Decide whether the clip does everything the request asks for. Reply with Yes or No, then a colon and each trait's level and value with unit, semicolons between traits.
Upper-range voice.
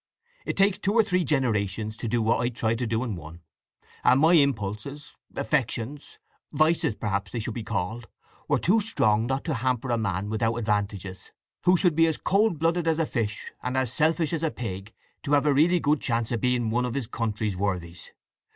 No: low, 120 Hz